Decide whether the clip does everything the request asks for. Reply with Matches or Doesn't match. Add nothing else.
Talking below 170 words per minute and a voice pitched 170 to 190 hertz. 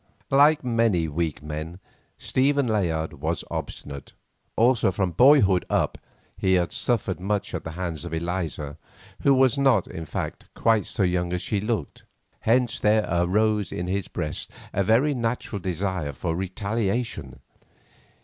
Doesn't match